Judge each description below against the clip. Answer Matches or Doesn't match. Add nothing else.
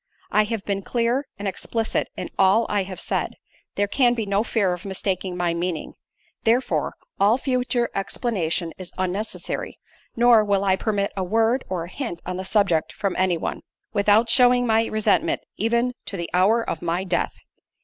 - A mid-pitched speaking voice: Doesn't match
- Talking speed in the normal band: Matches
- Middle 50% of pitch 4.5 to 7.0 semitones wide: Doesn't match